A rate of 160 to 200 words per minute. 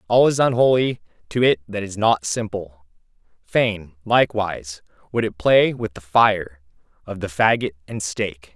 No: average, 145 wpm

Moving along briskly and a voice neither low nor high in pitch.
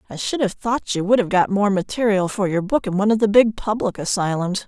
No: fast, 255 wpm; high, 200 Hz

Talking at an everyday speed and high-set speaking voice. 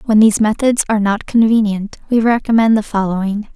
Yes: average, 170 wpm; high, 215 Hz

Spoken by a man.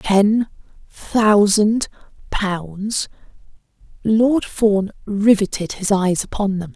No: female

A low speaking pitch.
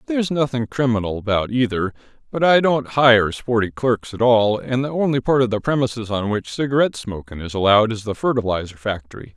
Yes: low, 120 Hz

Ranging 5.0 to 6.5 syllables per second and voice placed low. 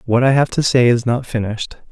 Yes: 6.0 syllables/s; low, 120 Hz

